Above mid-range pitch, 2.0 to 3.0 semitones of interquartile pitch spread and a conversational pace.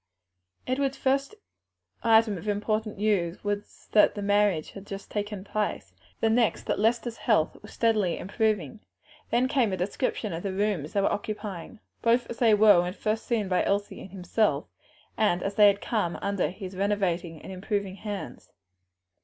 Yes: high, 205 Hz; average, 2.7 semitones; average, 165 wpm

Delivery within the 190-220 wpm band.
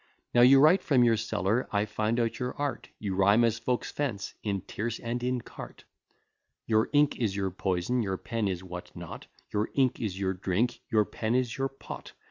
Yes: average, 200 wpm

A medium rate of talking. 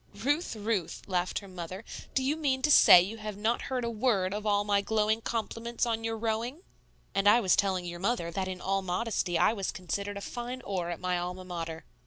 No: fast, 220 wpm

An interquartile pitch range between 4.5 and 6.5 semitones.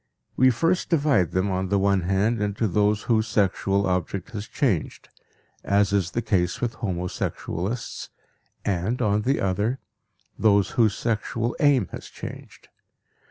No: average, 3.4 semitones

